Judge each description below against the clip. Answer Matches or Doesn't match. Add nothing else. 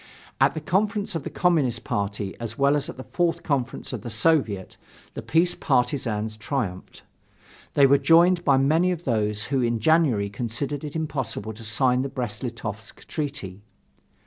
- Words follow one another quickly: Doesn't match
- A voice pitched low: Matches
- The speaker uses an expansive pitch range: Matches